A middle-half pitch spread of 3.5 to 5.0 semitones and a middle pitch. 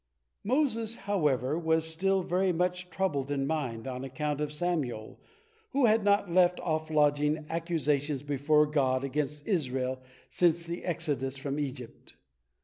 Yes: average, 4.4 semitones; medium, 150 Hz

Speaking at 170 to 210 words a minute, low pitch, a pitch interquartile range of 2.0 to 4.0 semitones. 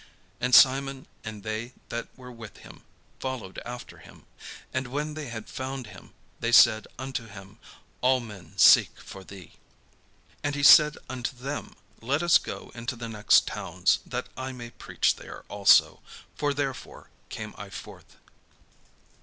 No: average, 155 wpm; low, 125 Hz; average, 3.3 semitones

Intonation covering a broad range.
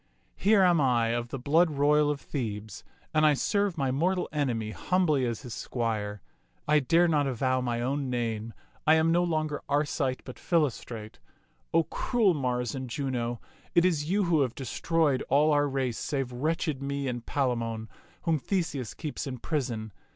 No: average, 4.4 semitones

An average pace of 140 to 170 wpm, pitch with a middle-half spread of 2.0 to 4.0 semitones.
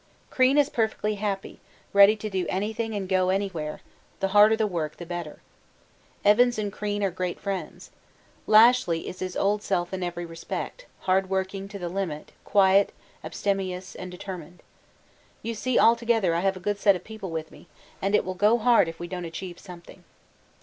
No: average, 180 wpm; average, 2.8 semitones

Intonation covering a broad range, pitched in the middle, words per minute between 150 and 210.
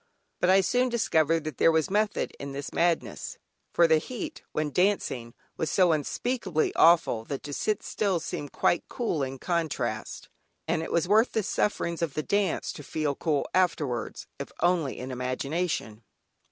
No: average, 4.6 semitones; medium, 165 Hz; average, 165 wpm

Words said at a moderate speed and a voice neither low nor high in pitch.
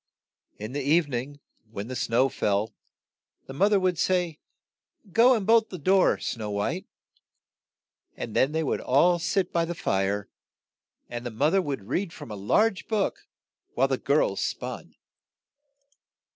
Yes: average, 160 wpm; medium, 150 Hz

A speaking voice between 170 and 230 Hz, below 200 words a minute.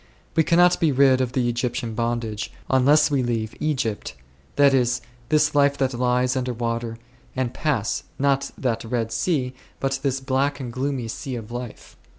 No: low, 130 Hz; average, 170 wpm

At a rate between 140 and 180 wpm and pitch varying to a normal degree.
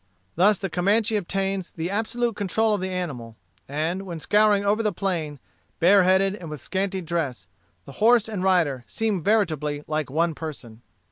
Yes: average, 160 wpm; average, 4.5 semitones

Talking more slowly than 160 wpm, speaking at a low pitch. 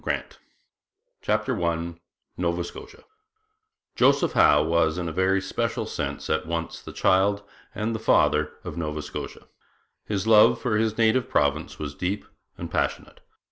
Yes: average, 140 wpm; very low, 95 Hz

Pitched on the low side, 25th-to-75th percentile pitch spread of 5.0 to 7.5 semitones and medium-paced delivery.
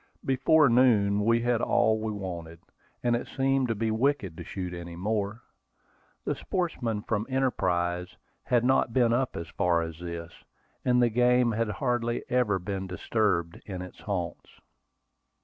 Yes: low, 110 Hz; average, 5.3 semitones; average, 155 wpm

